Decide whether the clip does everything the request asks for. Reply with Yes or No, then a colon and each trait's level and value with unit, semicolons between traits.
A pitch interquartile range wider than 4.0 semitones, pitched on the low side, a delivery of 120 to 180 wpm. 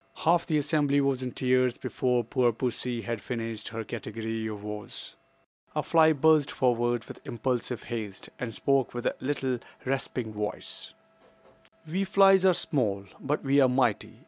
No: average, 3.7 semitones; low, 125 Hz; average, 155 wpm